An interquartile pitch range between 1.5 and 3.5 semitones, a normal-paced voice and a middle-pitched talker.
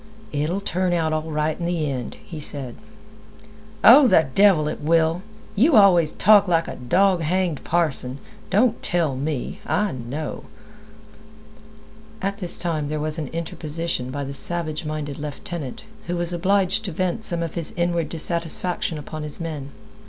Yes: average, 2.8 semitones; average, 160 wpm; medium, 165 Hz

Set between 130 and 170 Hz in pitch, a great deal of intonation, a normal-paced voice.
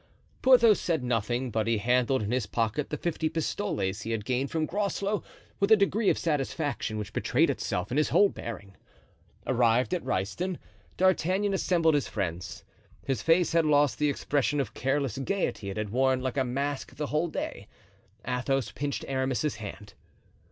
Yes: low, 135 Hz; wide, 6.0 semitones; average, 170 wpm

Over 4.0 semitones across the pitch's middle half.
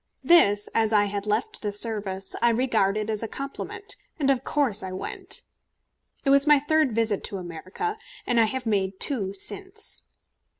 Yes: wide, 5.6 semitones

